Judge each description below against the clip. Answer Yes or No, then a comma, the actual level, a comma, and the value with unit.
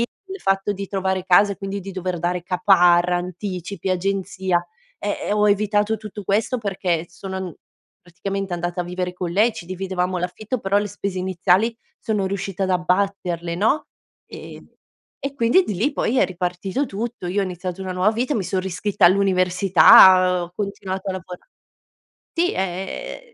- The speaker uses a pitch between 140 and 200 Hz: Yes, high, 190 Hz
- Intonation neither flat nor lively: No, narrow, 2.2 semitones